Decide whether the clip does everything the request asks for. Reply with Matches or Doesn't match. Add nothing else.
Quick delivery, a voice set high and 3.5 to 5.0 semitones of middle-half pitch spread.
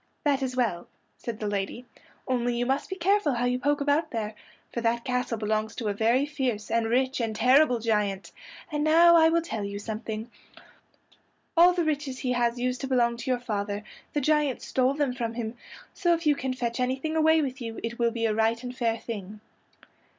Matches